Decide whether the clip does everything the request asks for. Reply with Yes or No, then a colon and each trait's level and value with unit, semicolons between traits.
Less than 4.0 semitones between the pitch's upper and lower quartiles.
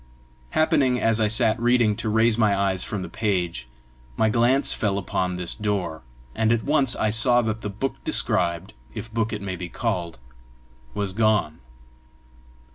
Yes: average, 3.6 semitones